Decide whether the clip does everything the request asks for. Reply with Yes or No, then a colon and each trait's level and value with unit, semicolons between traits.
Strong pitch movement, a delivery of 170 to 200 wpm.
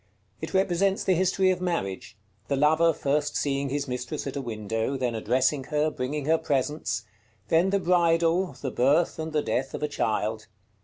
No: average, 4.3 semitones; average, 175 wpm